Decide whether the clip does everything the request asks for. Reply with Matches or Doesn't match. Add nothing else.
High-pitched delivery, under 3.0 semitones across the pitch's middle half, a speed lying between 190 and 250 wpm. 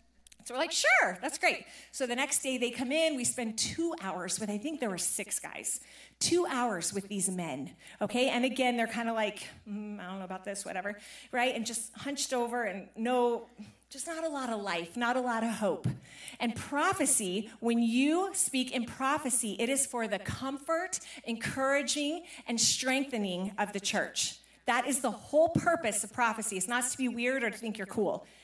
Doesn't match